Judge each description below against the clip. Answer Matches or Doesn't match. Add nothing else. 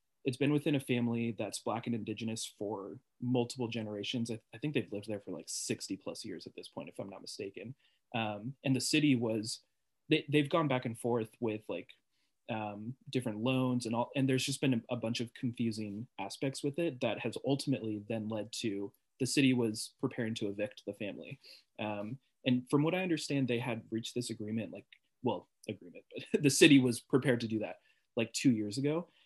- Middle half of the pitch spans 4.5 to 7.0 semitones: Doesn't match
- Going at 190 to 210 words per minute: Matches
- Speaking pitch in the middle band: Doesn't match